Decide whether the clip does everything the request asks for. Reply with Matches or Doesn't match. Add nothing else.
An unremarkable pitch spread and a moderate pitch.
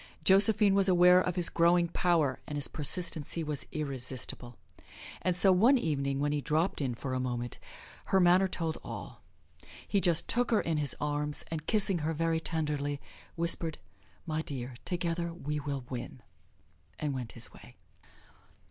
Matches